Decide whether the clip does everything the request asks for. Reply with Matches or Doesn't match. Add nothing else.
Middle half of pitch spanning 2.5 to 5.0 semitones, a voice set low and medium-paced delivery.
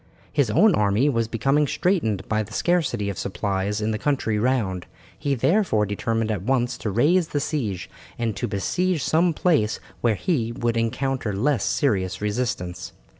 Doesn't match